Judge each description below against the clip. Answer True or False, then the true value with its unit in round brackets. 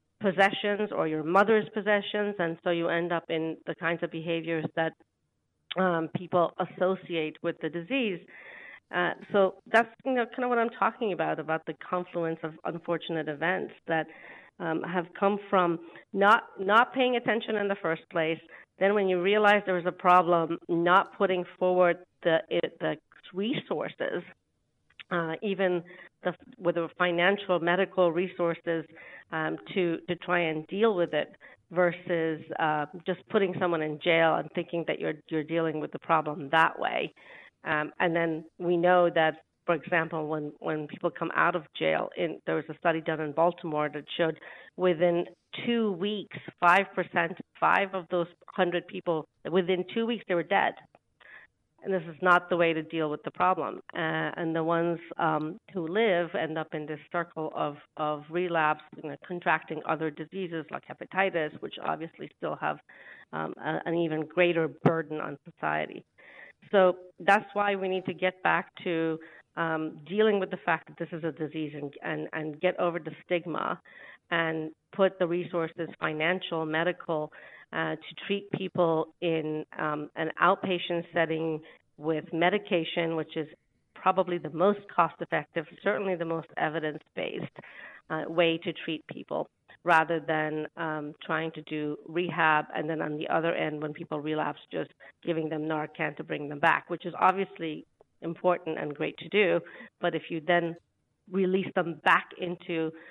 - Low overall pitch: False (170 Hz)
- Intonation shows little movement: True (2.3 semitones)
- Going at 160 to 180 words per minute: True (165 wpm)